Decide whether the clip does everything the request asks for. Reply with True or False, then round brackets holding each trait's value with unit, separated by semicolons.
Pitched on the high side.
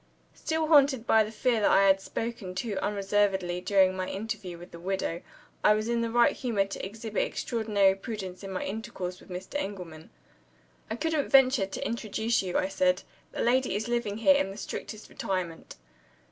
True (205 Hz)